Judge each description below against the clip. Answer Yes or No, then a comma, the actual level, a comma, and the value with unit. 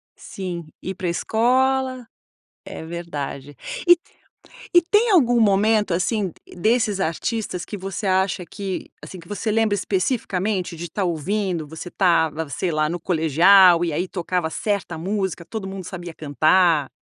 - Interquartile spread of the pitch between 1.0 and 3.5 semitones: No, average, 3.9 semitones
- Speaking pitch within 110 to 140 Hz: No, medium, 185 Hz